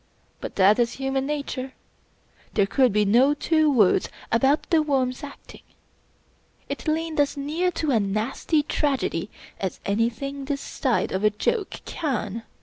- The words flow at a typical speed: Yes, average, 145 wpm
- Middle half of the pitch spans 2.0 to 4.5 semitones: No, average, 4.9 semitones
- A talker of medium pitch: No, very high, 270 Hz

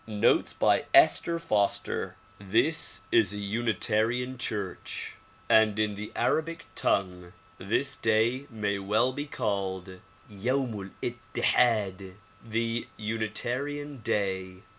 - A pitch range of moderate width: Yes, average, 3.3 semitones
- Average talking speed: No, slow, 95 wpm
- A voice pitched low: Yes, low, 110 Hz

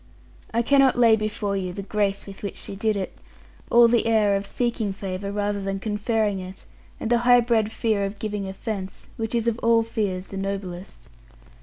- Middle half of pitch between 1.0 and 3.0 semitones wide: Yes, narrow, 2.6 semitones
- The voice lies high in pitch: Yes, high, 210 Hz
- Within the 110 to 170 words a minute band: No, average, 190 wpm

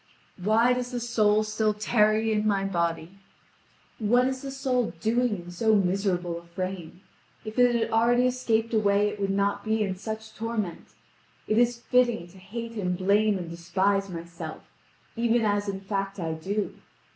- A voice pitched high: Yes, high, 210 Hz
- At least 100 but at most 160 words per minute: No, average, 170 wpm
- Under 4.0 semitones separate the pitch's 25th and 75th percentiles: Yes, average, 3.2 semitones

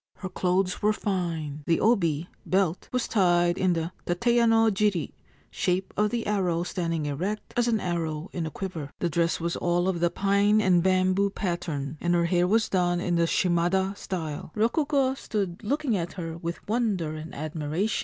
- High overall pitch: No, medium, 180 Hz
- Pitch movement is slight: No, average, 3.3 semitones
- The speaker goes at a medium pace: Yes, average, 175 wpm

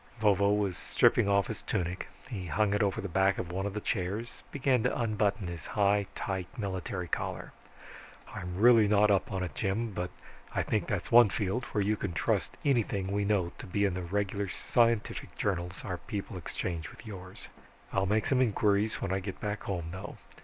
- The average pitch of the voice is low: Yes, low, 100 Hz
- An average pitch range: No, narrow, 2.3 semitones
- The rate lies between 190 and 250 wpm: Yes, average, 195 wpm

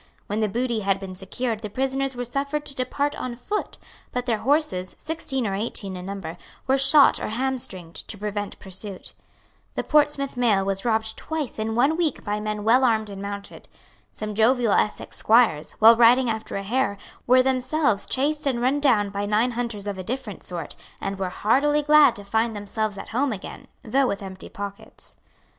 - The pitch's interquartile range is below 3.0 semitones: No, average, 4.7 semitones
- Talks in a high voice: Yes, high, 225 Hz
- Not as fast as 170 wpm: No, average, 190 wpm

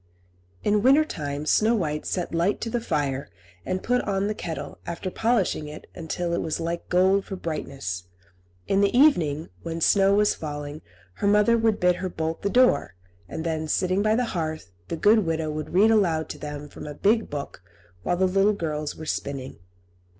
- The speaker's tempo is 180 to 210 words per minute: Yes, average, 190 wpm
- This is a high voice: No, medium, 175 Hz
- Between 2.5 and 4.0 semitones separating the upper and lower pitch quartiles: No, average, 5.1 semitones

